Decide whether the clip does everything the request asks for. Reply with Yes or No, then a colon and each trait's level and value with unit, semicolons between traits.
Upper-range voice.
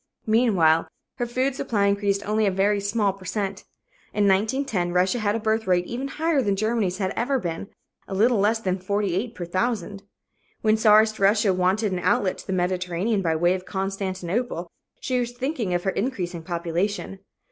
Yes: high, 200 Hz